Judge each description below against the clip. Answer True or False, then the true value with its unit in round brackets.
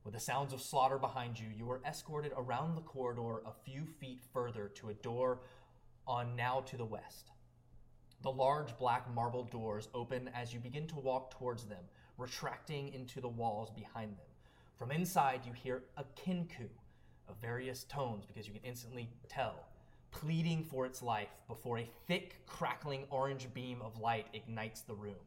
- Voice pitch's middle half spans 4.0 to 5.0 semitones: False (2.6 semitones)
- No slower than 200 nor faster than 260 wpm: False (175 wpm)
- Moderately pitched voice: False (125 Hz)